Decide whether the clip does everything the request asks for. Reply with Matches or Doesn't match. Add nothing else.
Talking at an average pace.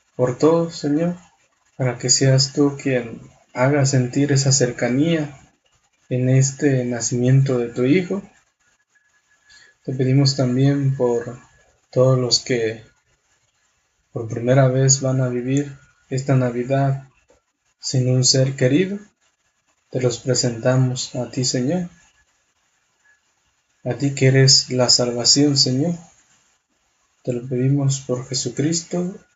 Doesn't match